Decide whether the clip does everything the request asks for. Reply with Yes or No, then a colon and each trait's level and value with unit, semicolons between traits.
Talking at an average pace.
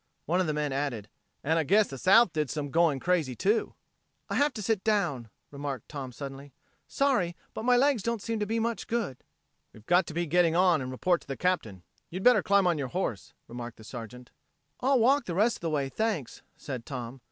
No: fast, 220 wpm